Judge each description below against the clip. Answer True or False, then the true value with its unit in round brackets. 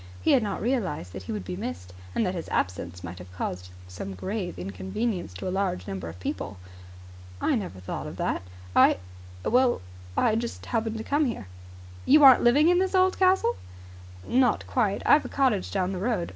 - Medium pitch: False (195 Hz)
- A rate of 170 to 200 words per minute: True (190 wpm)